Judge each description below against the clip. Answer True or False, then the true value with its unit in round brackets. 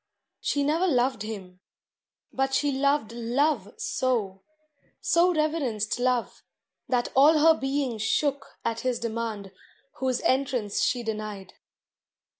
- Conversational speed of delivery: False (115 wpm)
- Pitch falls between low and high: False (250 Hz)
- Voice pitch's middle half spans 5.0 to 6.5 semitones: False (4.3 semitones)